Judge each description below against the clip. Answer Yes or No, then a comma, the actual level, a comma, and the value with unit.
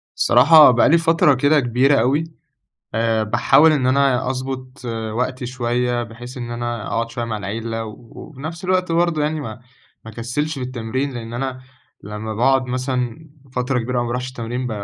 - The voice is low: Yes, low, 125 Hz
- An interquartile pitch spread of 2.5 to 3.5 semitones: Yes, average, 2.8 semitones